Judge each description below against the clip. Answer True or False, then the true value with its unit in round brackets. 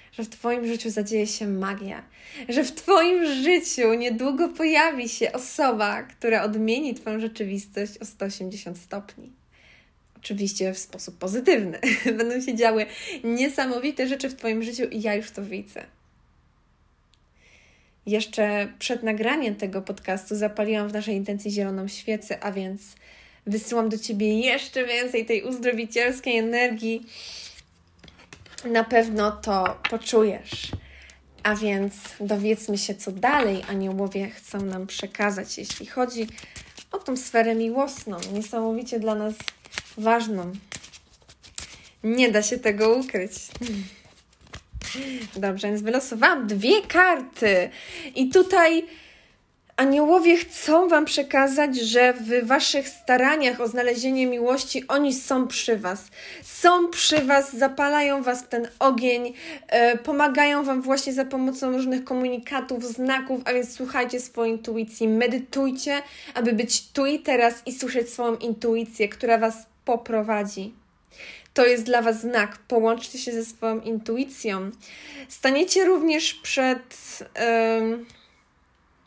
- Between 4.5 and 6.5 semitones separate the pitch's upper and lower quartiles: False (3.8 semitones)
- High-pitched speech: True (235 Hz)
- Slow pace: True (120 wpm)